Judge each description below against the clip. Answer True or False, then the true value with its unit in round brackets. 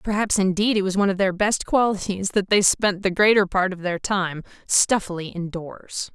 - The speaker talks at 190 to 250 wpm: True (195 wpm)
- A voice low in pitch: False (195 Hz)